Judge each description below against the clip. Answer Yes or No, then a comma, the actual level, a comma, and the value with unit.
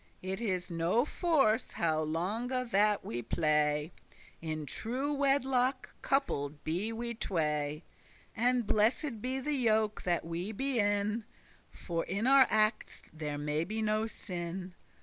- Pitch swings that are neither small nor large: No, wide, 6.7 semitones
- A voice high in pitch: Yes, high, 210 Hz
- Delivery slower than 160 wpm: Yes, average, 145 wpm